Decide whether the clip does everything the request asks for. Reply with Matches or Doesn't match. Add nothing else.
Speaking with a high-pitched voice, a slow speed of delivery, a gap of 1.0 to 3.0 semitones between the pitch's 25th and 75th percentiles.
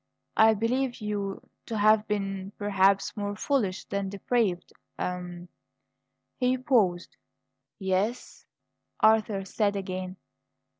Matches